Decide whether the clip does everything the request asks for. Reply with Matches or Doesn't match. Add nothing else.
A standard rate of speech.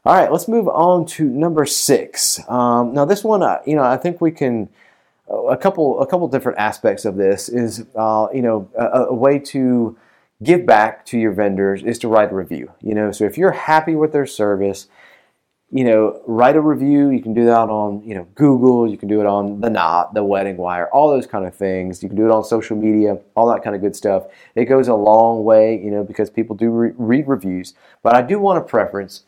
Doesn't match